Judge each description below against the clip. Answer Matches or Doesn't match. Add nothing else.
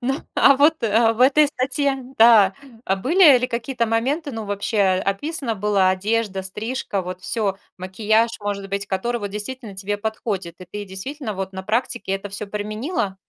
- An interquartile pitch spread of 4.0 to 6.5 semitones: Matches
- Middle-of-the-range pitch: Doesn't match